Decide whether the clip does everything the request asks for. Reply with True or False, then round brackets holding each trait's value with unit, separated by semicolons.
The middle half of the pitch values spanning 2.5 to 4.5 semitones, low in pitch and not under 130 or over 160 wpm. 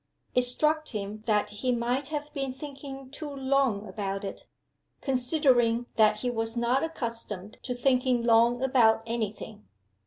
False (3.3 semitones; 245 Hz; 150 wpm)